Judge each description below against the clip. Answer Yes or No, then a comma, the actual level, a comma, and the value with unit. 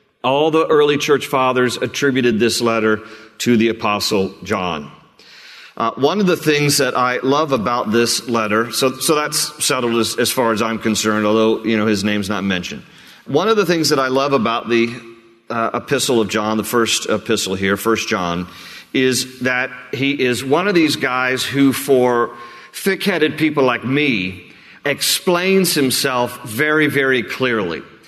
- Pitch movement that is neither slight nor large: Yes, average, 3.9 semitones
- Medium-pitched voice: No, low, 125 Hz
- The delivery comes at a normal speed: Yes, average, 165 wpm